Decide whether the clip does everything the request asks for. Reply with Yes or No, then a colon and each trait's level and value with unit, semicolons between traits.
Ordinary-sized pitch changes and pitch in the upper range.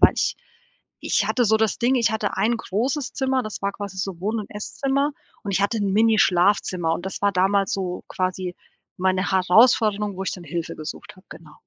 Yes: average, 3.0 semitones; high, 200 Hz